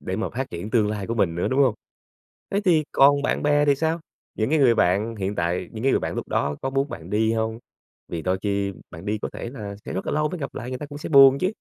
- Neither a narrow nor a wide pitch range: No, wide, 5.9 semitones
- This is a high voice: No, low, 115 Hz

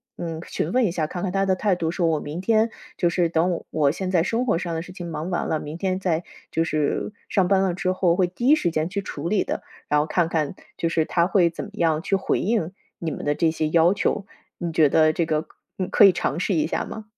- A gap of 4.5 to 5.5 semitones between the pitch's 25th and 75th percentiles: No, average, 2.9 semitones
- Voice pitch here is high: No, medium, 170 Hz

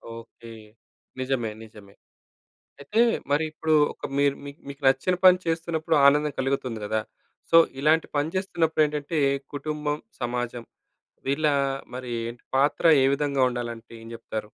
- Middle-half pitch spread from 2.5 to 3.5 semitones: No, average, 4.4 semitones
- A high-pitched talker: No, medium, 140 Hz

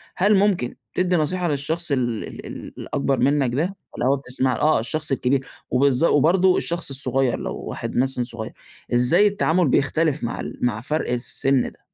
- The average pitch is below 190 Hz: Yes, medium, 140 Hz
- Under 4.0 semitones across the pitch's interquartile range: No, average, 4.8 semitones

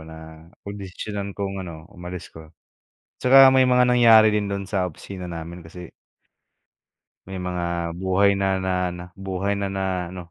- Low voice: Yes, very low, 95 Hz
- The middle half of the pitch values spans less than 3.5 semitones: Yes, narrow, 2.4 semitones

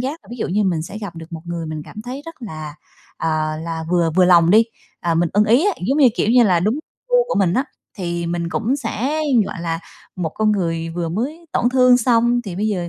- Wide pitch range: Yes, wide, 6.3 semitones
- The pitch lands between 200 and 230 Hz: No, high, 190 Hz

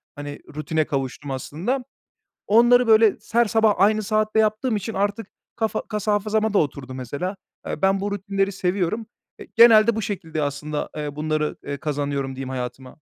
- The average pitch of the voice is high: Yes, high, 195 Hz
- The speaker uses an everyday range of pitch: No, wide, 6.9 semitones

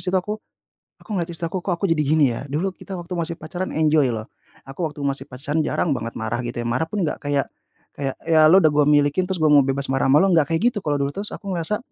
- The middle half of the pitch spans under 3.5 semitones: No, average, 4.0 semitones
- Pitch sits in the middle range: Yes, medium, 155 Hz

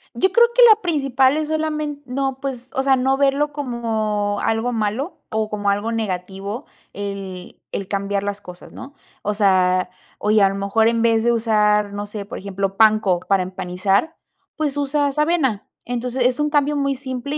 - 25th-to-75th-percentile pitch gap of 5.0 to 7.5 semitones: Yes, wide, 5.5 semitones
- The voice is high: Yes, high, 230 Hz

